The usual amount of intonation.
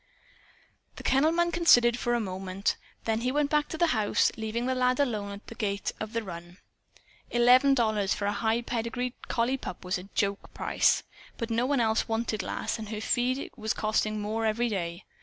Yes: average, 3.2 semitones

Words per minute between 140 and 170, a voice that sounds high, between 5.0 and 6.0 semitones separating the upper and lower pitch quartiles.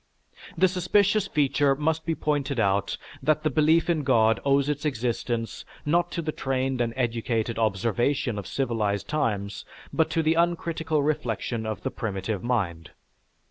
No: average, 150 wpm; low, 135 Hz; wide, 5.5 semitones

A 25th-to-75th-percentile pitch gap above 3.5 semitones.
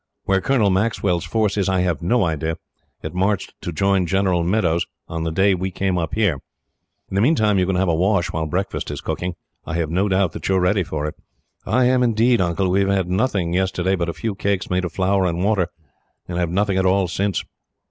No: narrow, 2.4 semitones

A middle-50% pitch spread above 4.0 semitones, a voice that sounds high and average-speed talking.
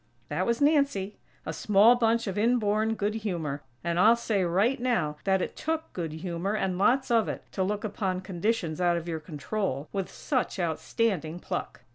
Yes: average, 4.7 semitones; high, 195 Hz; average, 185 wpm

